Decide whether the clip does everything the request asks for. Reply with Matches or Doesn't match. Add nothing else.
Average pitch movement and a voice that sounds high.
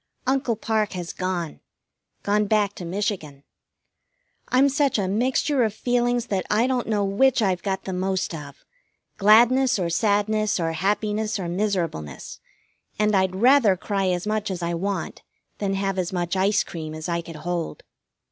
Matches